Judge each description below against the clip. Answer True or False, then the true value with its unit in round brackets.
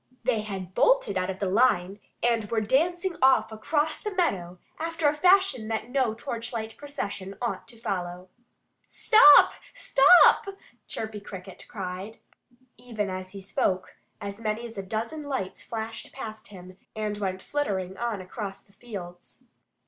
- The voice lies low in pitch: False (220 Hz)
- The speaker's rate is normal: True (150 wpm)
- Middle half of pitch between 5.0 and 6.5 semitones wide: True (5.5 semitones)